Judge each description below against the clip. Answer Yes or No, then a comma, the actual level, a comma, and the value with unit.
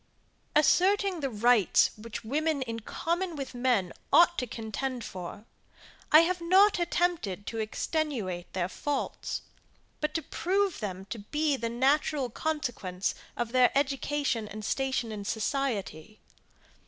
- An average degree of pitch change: No, wide, 6.3 semitones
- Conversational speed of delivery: No, slow, 130 wpm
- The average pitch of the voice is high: Yes, very high, 260 Hz